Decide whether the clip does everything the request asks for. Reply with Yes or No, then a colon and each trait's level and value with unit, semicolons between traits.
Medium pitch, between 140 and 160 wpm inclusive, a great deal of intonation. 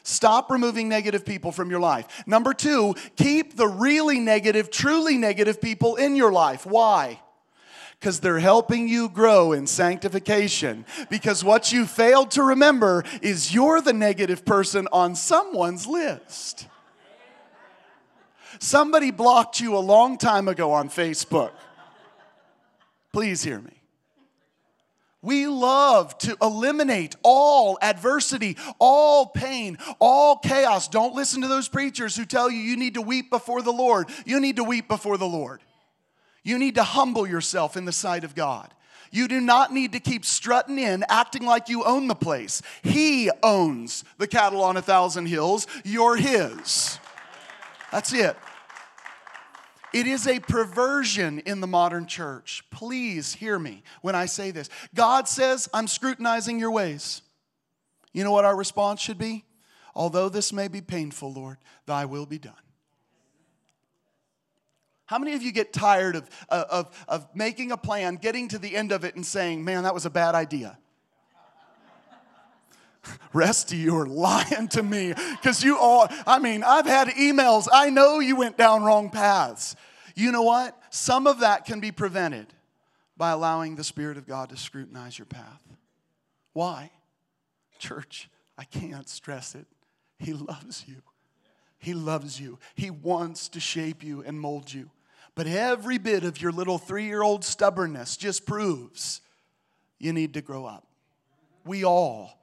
No: high, 205 Hz; average, 150 wpm; wide, 6.4 semitones